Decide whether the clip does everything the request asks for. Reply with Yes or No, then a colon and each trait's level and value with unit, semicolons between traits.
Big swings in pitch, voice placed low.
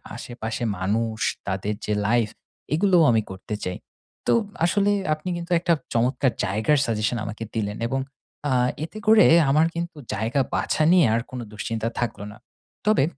Yes: wide, 7.1 semitones; low, 120 Hz